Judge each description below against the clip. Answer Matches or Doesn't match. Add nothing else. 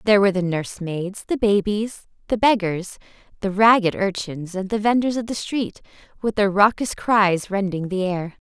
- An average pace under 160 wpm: Matches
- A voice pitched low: Doesn't match